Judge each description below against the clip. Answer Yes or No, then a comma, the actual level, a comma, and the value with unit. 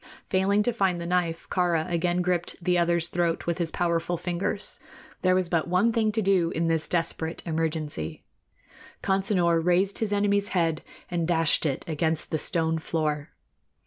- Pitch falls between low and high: Yes, medium, 170 Hz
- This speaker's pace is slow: No, average, 165 wpm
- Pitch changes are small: Yes, narrow, 2.1 semitones